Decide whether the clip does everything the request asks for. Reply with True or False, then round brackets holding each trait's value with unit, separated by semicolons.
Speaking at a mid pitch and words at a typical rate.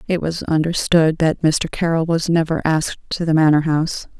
True (160 Hz; 185 wpm)